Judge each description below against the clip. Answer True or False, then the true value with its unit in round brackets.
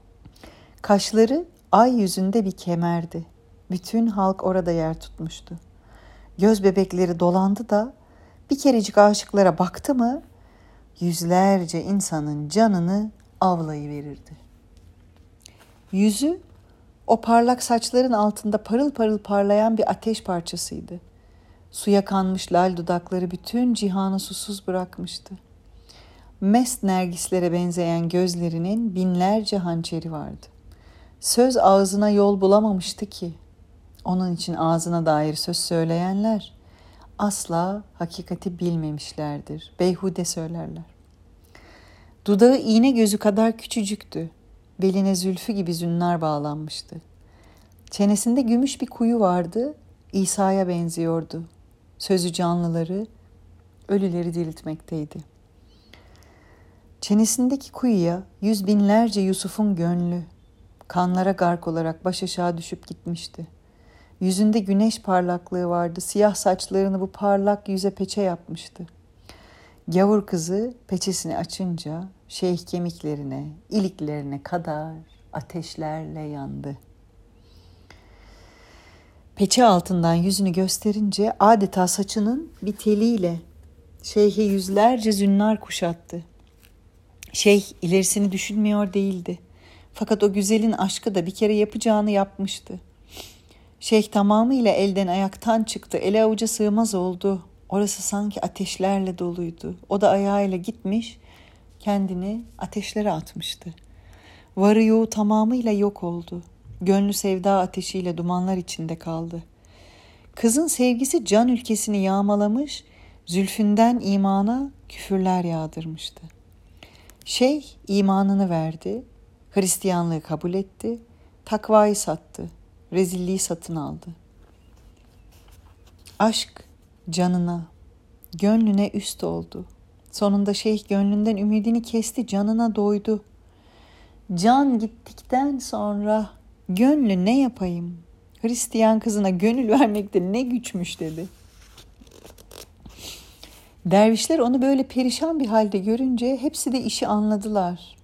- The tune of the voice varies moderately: True (4.9 semitones)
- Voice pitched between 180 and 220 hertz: True (185 Hz)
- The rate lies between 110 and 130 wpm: False (95 wpm)